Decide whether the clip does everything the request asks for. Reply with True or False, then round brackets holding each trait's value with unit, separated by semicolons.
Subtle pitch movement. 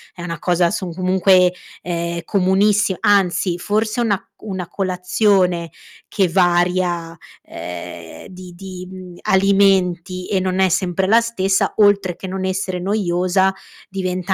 True (1.6 semitones)